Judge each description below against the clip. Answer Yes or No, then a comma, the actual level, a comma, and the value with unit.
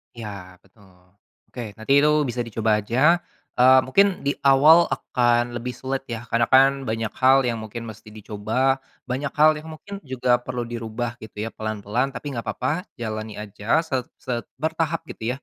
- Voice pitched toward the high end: No, low, 120 Hz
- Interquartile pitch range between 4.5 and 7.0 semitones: No, average, 3.6 semitones